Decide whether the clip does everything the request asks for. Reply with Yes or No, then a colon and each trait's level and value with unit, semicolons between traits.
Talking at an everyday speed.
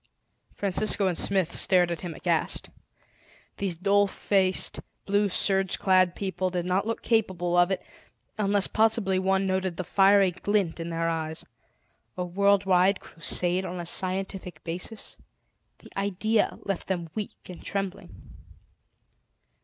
No: slow, 130 wpm